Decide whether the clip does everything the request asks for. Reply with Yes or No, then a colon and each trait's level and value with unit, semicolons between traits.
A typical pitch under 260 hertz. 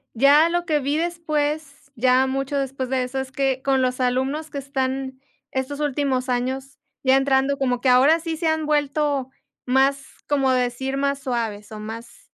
No: very high, 270 Hz